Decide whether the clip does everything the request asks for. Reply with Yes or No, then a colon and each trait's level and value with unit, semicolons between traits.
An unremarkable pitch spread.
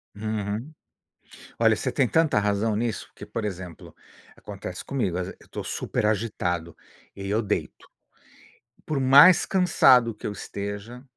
Yes: average, 3.5 semitones